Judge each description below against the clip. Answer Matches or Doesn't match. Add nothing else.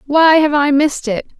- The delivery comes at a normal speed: Doesn't match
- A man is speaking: Doesn't match